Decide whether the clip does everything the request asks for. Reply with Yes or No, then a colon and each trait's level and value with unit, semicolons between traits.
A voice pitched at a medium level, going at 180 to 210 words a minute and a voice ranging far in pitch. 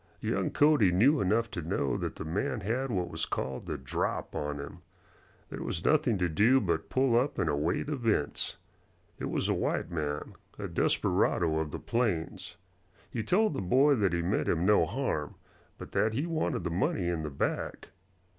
No: very low, 95 Hz; average, 185 wpm; wide, 7.3 semitones